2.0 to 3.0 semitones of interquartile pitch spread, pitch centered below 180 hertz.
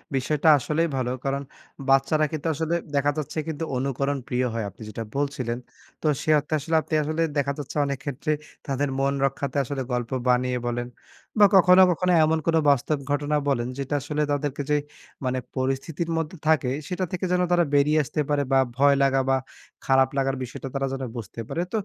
Yes: average, 2.7 semitones; medium, 140 Hz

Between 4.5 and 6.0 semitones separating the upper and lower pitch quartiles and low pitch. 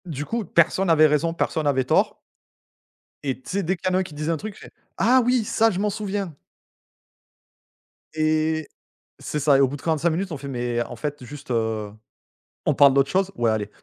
No: average, 5.3 semitones; medium, 155 Hz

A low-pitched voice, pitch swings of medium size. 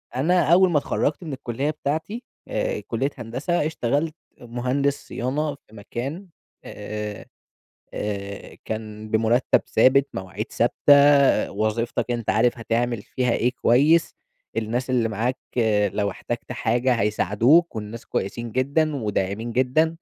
Yes: low, 120 Hz; average, 4.5 semitones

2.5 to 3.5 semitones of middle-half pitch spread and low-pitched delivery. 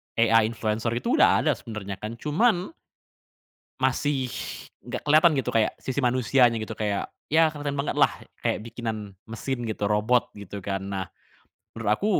No: average, 4.3 semitones; low, 115 Hz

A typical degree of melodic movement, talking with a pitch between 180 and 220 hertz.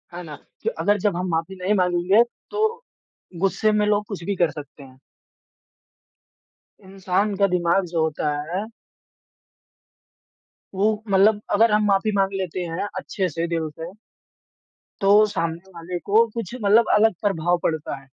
Yes: average, 3.4 semitones; high, 190 Hz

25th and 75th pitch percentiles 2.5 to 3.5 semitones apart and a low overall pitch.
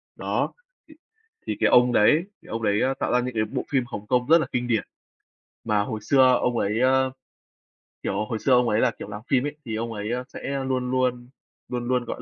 Yes: average, 2.8 semitones; low, 125 Hz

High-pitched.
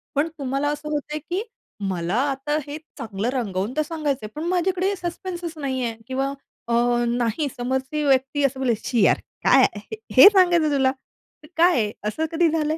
Yes: very high, 280 Hz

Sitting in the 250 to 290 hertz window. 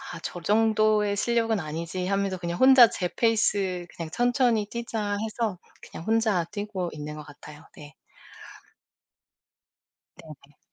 No: high, 200 Hz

